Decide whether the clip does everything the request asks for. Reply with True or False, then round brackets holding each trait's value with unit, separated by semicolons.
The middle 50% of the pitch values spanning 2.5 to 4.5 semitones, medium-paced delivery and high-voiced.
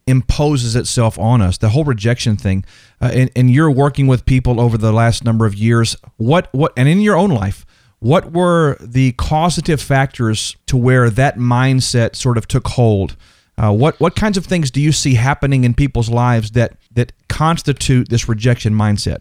False (3.7 semitones; 185 wpm; 125 Hz)